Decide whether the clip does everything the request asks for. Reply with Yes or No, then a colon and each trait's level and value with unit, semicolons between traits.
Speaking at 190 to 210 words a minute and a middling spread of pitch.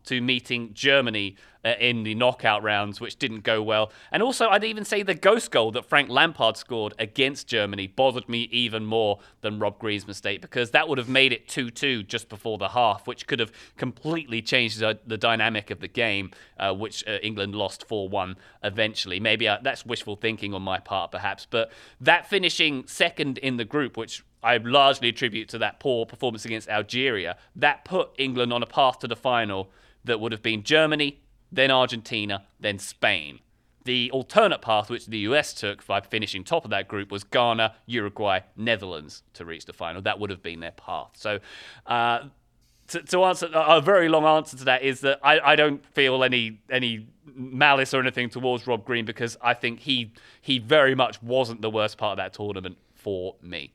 Yes: average, 195 wpm; average, 3.7 semitones